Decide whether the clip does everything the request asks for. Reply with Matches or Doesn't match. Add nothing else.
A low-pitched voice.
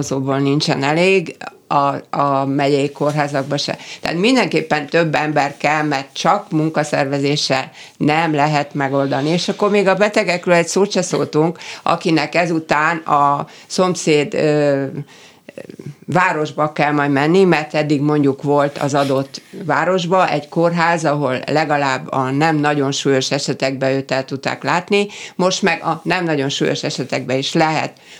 Doesn't match